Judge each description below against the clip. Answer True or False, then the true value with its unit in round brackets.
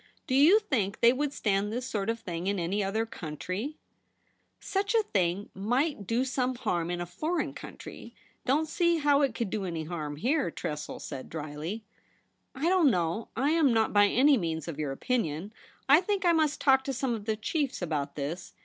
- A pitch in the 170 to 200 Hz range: False (225 Hz)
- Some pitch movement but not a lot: False (8.3 semitones)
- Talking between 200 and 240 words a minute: True (205 wpm)